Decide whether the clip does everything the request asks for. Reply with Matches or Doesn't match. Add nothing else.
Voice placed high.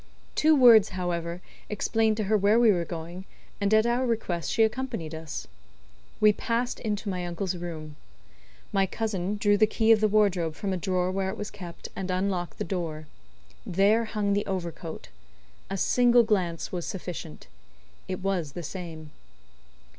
Matches